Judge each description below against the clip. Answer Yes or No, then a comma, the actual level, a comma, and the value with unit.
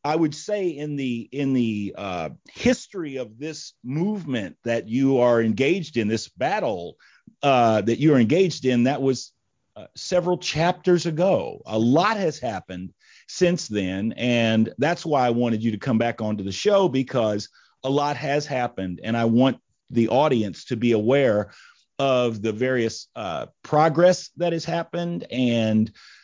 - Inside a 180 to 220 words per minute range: No, average, 160 wpm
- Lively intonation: Yes, wide, 5.9 semitones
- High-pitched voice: No, low, 130 Hz